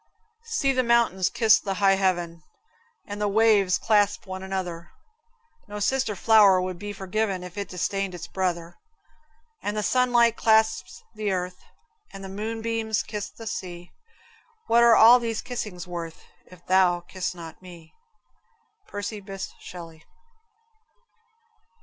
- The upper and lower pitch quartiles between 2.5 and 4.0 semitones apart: Yes, average, 3.4 semitones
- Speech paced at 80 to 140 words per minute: Yes, slow, 135 wpm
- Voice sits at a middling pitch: No, high, 195 Hz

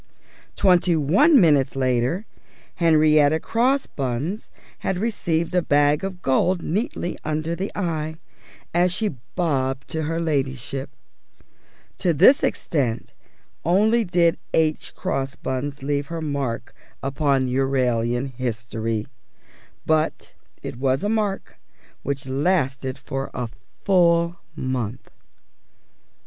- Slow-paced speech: Yes, slow, 105 wpm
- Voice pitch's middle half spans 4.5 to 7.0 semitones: Yes, average, 4.8 semitones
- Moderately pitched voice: Yes, medium, 150 Hz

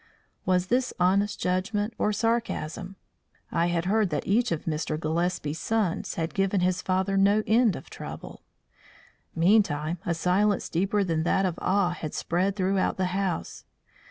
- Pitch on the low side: No, medium, 185 Hz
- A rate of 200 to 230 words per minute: No, average, 155 wpm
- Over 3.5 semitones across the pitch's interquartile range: No, average, 3.2 semitones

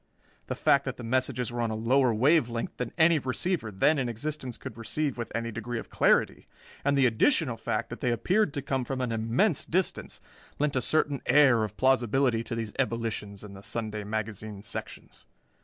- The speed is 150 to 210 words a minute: Yes, average, 195 wpm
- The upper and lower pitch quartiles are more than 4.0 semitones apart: No, average, 3.6 semitones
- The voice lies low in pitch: Yes, low, 120 Hz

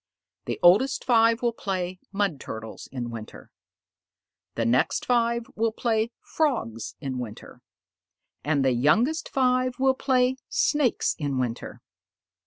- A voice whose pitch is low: No, high, 215 Hz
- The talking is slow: Yes, slow, 125 wpm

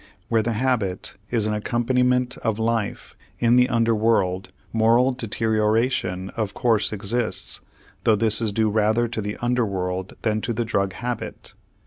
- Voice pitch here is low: Yes, low, 110 Hz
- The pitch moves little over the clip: Yes, narrow, 2.3 semitones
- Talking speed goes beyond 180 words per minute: No, average, 155 wpm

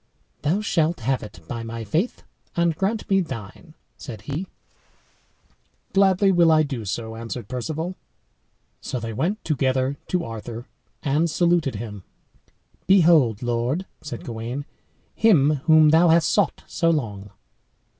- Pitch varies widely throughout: Yes, wide, 6.6 semitones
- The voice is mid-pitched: Yes, medium, 145 Hz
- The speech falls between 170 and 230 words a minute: No, slow, 135 wpm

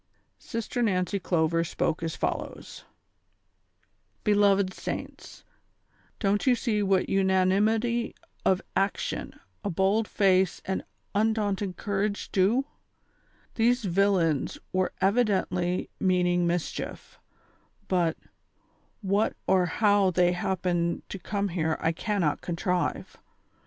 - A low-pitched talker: No, high, 190 Hz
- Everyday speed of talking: No, slow, 105 wpm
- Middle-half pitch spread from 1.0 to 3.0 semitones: Yes, narrow, 2.6 semitones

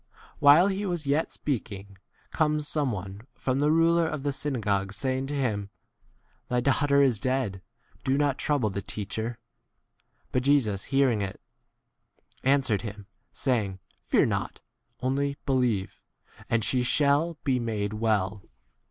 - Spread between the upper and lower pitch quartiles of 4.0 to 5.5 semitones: Yes, average, 5.2 semitones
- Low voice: Yes, low, 130 Hz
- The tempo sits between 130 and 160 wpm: Yes, average, 145 wpm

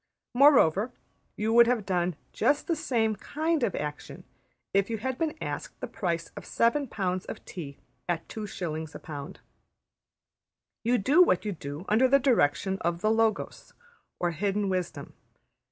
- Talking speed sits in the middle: Yes, average, 155 wpm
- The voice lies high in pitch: Yes, high, 205 Hz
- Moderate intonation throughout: No, wide, 5.7 semitones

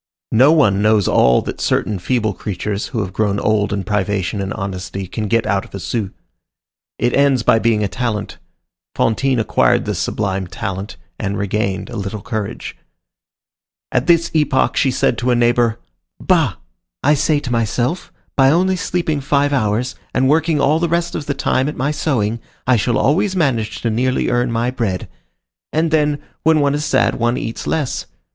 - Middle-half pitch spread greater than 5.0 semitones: Yes, wide, 5.5 semitones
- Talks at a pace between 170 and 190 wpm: Yes, average, 180 wpm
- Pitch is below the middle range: Yes, low, 120 Hz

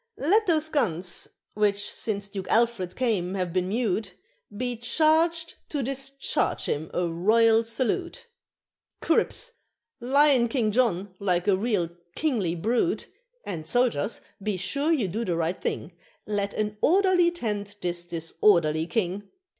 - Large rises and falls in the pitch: Yes, wide, 6.3 semitones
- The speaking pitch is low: No, high, 215 Hz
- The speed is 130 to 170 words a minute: Yes, slow, 135 wpm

